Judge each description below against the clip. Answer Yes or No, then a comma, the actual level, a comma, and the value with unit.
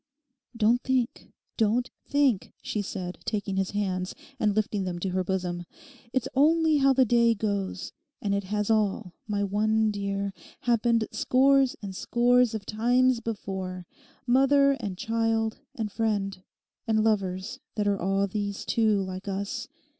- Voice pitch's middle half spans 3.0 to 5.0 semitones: Yes, average, 3.3 semitones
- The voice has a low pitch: No, high, 210 Hz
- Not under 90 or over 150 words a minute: Yes, average, 140 wpm